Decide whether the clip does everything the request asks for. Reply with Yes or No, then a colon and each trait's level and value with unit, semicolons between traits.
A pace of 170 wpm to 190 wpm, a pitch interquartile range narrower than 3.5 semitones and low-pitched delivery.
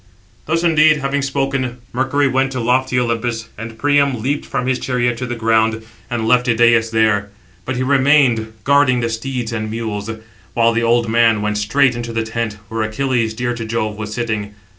Yes: average, 185 wpm; average, 2.8 semitones; low, 120 Hz